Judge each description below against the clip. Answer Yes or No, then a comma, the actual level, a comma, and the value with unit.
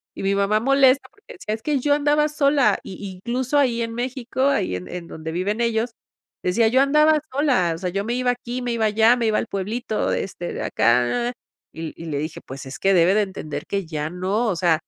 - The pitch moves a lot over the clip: Yes, wide, 5.9 semitones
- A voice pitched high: Yes, high, 220 Hz